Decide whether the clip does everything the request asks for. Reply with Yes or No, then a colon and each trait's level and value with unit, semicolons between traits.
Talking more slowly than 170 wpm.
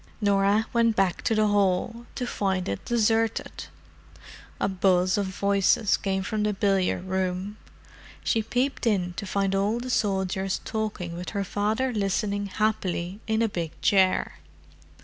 Yes: average, 145 wpm